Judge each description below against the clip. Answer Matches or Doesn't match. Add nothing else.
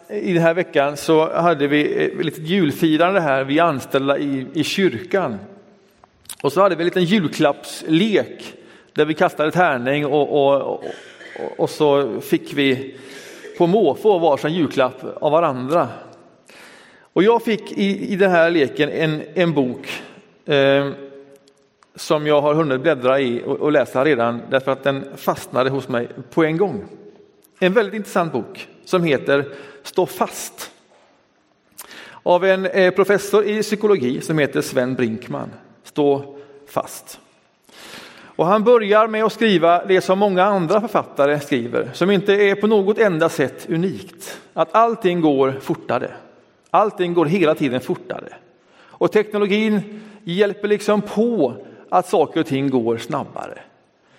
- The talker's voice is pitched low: Doesn't match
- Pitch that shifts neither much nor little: Doesn't match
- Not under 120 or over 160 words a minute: Matches